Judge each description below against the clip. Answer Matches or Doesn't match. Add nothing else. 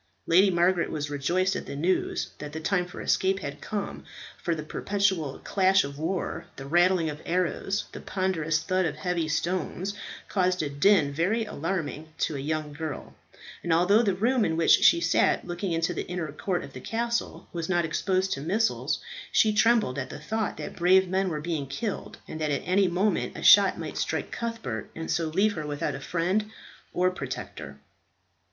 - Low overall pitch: Doesn't match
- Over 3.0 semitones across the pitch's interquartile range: Matches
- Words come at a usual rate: Matches